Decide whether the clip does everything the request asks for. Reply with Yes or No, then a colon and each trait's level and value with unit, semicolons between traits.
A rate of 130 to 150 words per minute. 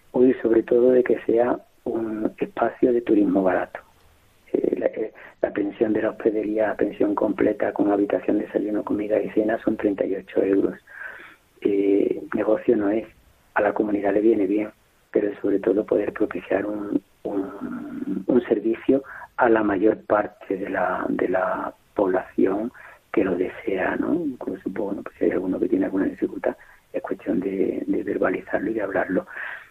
No: average, 165 wpm